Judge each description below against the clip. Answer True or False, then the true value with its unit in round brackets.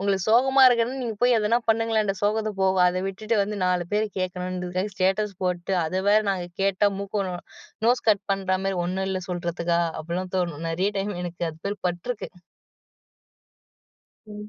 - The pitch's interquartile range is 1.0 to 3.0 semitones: True (2.7 semitones)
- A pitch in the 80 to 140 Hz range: False (195 Hz)